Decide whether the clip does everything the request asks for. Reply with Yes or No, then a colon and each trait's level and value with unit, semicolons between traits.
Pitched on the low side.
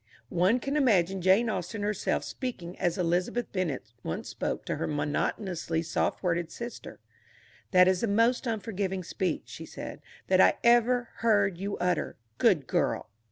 No: high, 190 Hz